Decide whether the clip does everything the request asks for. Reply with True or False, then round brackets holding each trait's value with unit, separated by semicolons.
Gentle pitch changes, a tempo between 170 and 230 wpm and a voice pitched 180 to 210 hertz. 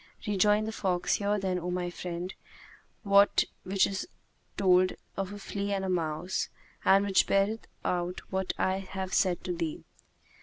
False (1.8 semitones; 160 wpm; 190 Hz)